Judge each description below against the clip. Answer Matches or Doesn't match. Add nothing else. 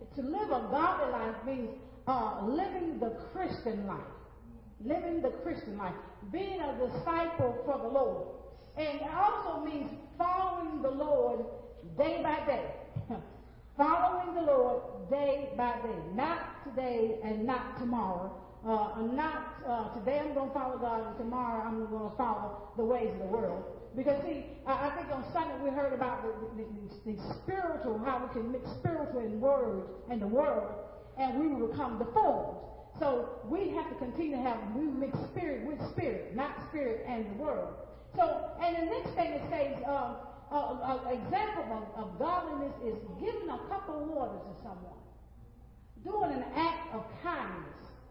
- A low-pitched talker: Doesn't match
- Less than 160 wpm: Doesn't match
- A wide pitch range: Matches